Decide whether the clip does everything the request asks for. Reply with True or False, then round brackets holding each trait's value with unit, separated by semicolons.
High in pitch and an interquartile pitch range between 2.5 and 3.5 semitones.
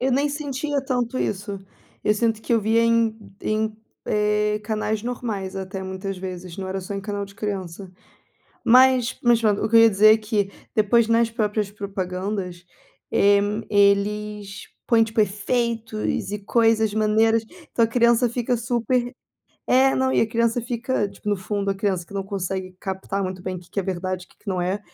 True (210 Hz; 2.8 semitones)